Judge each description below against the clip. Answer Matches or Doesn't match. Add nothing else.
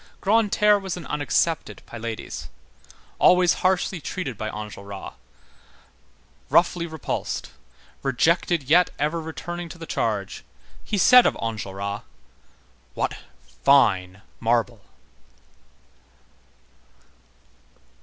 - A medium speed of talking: Doesn't match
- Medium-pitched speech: Matches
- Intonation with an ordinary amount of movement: Doesn't match